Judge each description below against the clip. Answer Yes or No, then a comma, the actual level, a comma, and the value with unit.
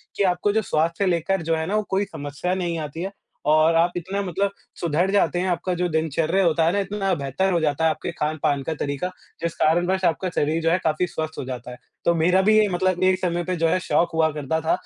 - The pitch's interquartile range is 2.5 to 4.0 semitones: Yes, average, 2.9 semitones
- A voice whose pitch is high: No, medium, 170 Hz